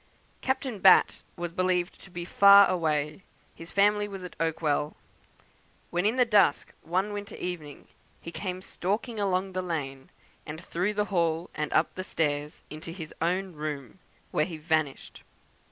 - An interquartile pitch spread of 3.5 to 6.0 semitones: Yes, average, 3.8 semitones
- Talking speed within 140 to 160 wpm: Yes, average, 155 wpm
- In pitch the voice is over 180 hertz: No, medium, 175 Hz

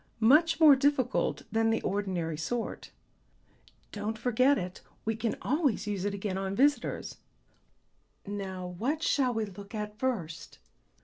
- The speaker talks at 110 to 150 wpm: Yes, slow, 135 wpm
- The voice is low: No, high, 220 Hz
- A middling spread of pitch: Yes, average, 4.7 semitones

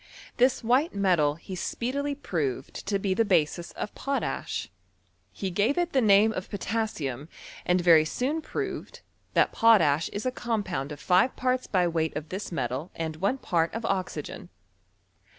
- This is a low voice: No, high, 190 Hz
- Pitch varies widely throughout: Yes, wide, 6.2 semitones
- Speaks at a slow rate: No, average, 160 wpm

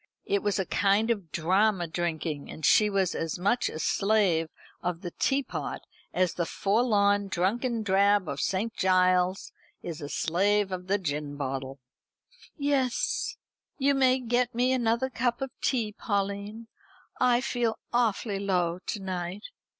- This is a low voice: No, high, 200 Hz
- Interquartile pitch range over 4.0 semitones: Yes, average, 4.7 semitones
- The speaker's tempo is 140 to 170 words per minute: Yes, average, 145 wpm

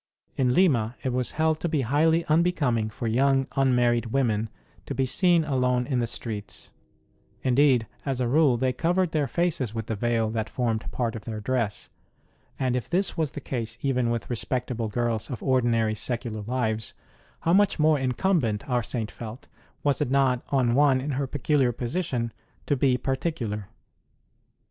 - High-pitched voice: No, low, 125 Hz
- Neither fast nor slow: Yes, average, 170 wpm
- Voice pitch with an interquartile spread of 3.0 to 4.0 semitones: Yes, average, 3.5 semitones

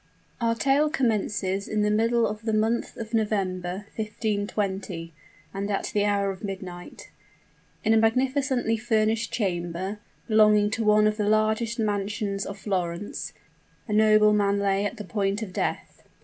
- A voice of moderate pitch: No, high, 210 Hz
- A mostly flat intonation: Yes, narrow, 2.0 semitones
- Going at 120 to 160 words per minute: Yes, average, 150 wpm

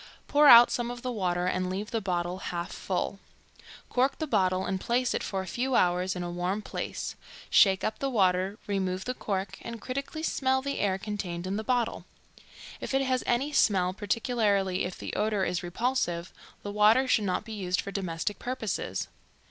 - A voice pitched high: Yes, high, 205 Hz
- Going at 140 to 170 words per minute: No, average, 190 wpm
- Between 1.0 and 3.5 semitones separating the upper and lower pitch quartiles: No, average, 4.7 semitones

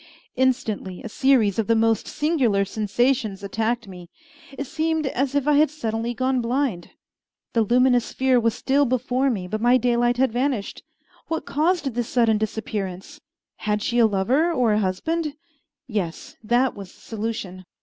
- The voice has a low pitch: No, high, 240 Hz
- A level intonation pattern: No, average, 3.8 semitones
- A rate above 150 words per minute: Yes, average, 160 wpm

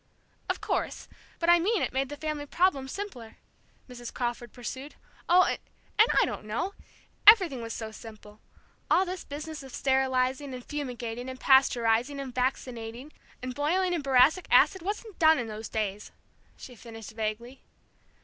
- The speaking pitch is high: Yes, very high, 265 Hz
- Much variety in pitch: No, average, 4.9 semitones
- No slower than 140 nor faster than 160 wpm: Yes, average, 155 wpm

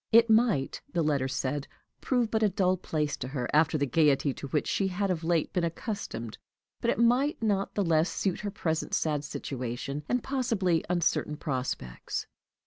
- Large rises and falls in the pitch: Yes, wide, 6.3 semitones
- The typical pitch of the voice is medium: Yes, medium, 165 Hz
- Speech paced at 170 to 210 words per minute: Yes, average, 180 wpm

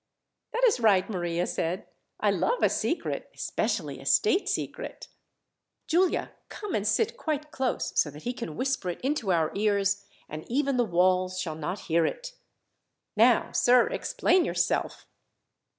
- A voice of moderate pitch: No, high, 215 Hz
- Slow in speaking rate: No, average, 150 wpm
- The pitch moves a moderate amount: No, wide, 9.0 semitones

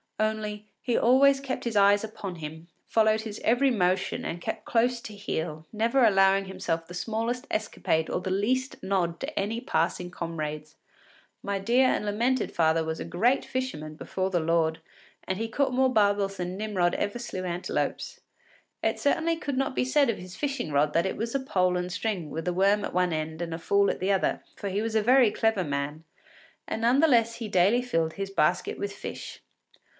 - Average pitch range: Yes, average, 4.9 semitones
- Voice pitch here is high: Yes, high, 200 Hz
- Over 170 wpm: Yes, average, 200 wpm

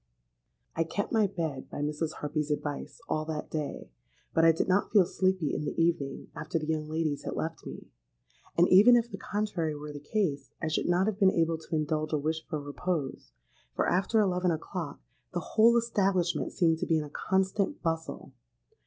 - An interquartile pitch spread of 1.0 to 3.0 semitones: No, average, 3.7 semitones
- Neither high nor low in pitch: Yes, medium, 165 Hz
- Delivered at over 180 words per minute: Yes, average, 190 wpm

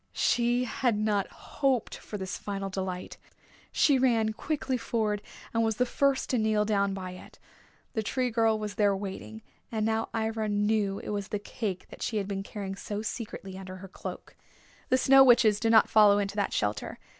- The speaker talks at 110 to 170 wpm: No, average, 190 wpm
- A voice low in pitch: No, high, 215 Hz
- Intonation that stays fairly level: Yes, narrow, 2.3 semitones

